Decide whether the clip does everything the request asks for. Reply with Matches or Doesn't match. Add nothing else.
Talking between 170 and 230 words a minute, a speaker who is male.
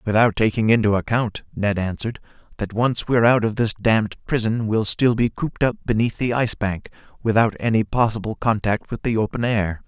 Matches